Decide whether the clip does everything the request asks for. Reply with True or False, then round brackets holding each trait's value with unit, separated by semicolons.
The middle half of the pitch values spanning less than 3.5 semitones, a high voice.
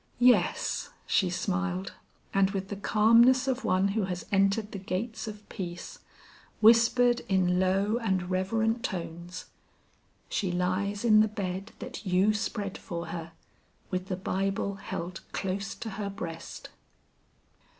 True (2.7 semitones; 195 Hz)